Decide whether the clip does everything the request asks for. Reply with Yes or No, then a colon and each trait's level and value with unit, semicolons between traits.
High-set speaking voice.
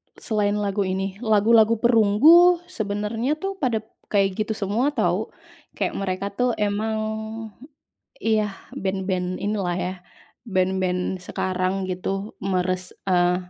Yes: high, 200 Hz